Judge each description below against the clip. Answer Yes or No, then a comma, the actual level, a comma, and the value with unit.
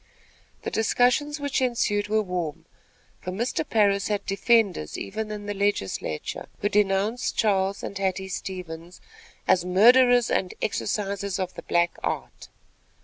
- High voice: Yes, high, 200 Hz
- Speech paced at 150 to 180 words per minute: No, slow, 135 wpm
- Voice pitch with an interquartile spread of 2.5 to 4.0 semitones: Yes, average, 2.9 semitones